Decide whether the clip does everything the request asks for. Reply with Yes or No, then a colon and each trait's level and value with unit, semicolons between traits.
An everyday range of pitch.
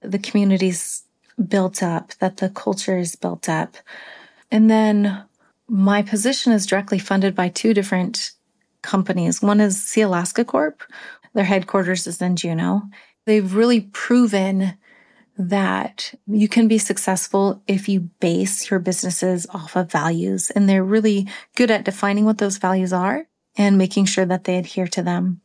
No: narrow, 2.3 semitones